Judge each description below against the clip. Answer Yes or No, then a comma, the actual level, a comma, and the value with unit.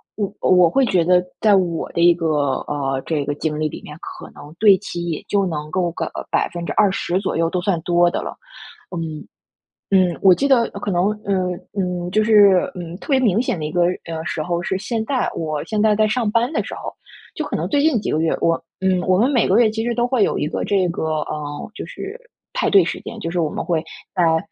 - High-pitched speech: No, medium, 180 Hz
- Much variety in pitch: No, average, 4.2 semitones